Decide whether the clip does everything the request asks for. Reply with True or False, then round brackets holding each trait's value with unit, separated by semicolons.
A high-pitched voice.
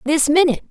True (305 Hz)